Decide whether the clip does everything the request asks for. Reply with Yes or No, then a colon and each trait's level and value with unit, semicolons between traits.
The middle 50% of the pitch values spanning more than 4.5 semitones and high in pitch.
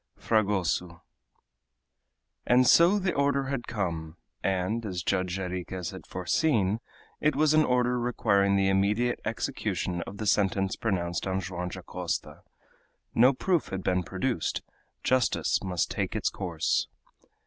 No: average, 5.2 semitones; low, 100 Hz